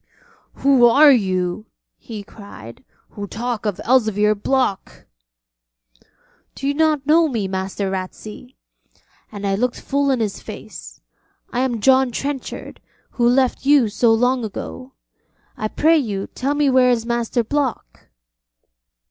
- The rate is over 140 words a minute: No, slow, 135 wpm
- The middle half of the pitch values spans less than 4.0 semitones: No, average, 4.3 semitones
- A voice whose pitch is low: No, high, 240 Hz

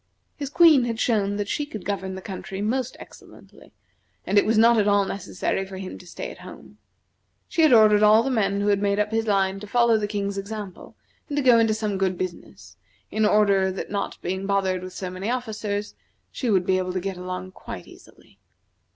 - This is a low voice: No, high, 205 Hz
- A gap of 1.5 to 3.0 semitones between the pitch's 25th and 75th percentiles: Yes, narrow, 2.6 semitones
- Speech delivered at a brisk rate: Yes, fast, 215 wpm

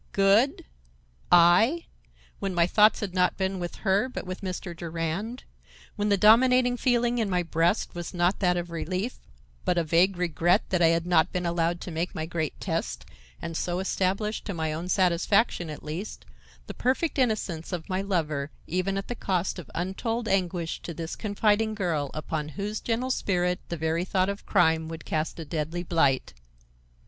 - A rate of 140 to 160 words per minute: No, average, 180 wpm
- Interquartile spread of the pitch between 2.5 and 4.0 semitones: Yes, average, 3.5 semitones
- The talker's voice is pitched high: No, medium, 180 Hz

